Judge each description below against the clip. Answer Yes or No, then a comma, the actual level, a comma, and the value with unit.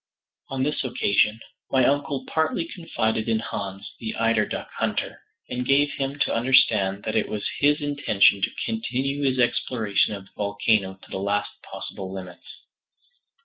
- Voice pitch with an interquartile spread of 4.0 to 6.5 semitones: Yes, average, 5.1 semitones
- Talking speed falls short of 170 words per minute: Yes, average, 155 wpm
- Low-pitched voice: Yes, low, 115 Hz